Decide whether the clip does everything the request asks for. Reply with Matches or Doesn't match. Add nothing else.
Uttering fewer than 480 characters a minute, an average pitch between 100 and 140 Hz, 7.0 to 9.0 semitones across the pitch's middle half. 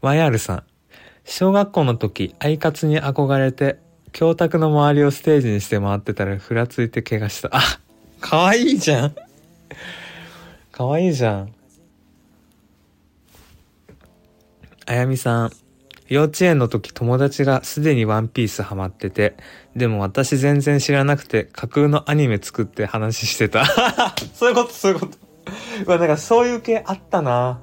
Doesn't match